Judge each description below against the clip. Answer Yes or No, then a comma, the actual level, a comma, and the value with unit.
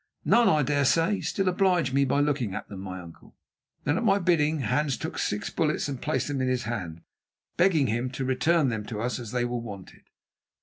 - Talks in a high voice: No, low, 135 Hz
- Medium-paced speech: No, fast, 215 wpm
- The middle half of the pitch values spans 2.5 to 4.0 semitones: No, average, 5.1 semitones